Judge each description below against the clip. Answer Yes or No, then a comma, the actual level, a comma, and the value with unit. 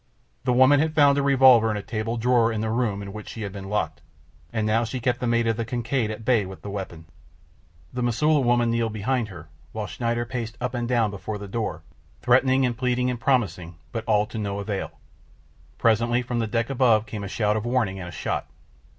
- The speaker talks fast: Yes, fast, 225 wpm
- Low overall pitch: Yes, low, 115 Hz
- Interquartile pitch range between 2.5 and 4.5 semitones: Yes, average, 2.8 semitones